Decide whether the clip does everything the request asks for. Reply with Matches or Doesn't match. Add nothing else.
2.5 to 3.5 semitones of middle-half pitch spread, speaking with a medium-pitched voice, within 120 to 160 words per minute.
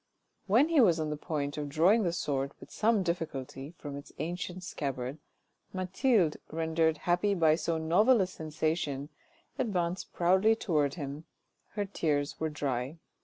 Doesn't match